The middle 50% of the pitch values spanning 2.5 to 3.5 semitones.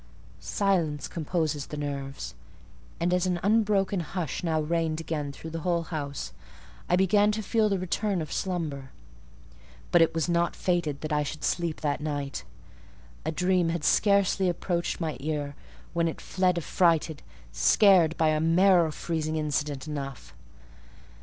Yes: average, 3.1 semitones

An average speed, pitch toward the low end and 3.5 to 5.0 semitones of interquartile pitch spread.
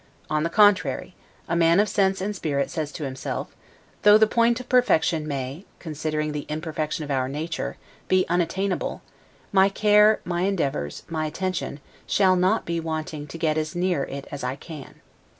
No: average, 170 wpm; medium, 165 Hz; average, 4.0 semitones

